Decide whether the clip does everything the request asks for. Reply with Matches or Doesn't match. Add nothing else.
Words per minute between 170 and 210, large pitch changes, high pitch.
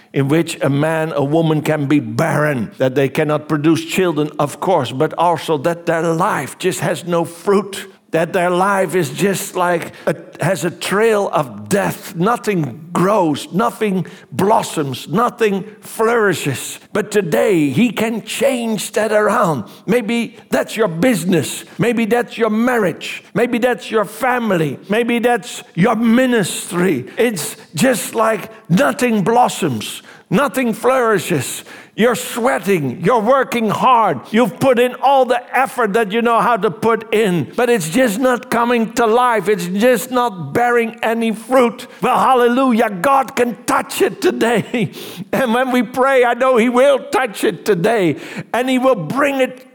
Doesn't match